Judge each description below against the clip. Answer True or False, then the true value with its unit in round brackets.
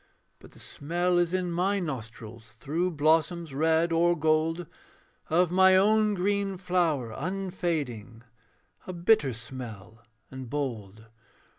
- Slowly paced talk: True (120 wpm)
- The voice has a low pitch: False (165 Hz)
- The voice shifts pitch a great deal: True (5.7 semitones)